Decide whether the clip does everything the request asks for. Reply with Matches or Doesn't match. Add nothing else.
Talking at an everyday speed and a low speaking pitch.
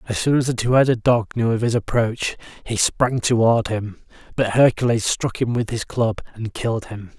Doesn't match